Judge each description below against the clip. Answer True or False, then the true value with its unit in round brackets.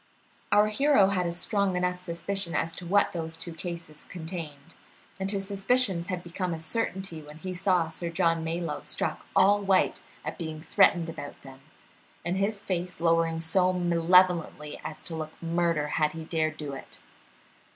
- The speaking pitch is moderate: True (170 Hz)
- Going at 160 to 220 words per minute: True (170 wpm)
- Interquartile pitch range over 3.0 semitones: False (2.7 semitones)